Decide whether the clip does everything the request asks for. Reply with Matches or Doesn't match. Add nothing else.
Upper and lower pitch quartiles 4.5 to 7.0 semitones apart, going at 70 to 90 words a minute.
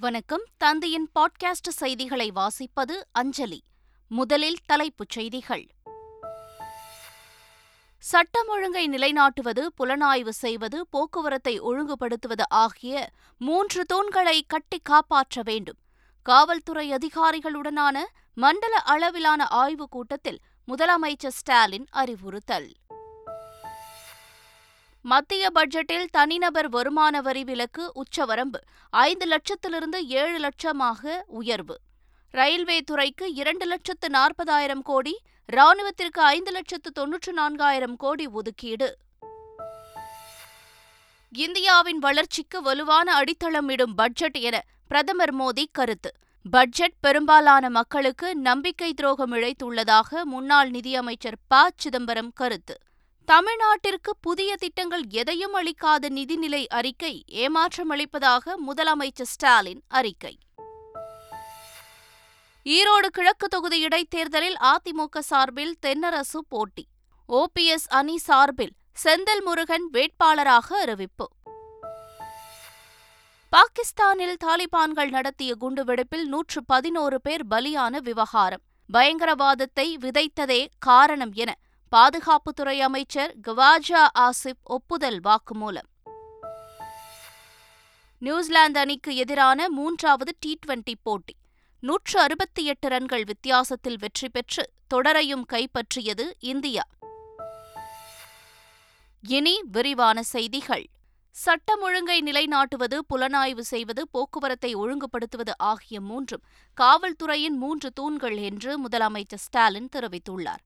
Matches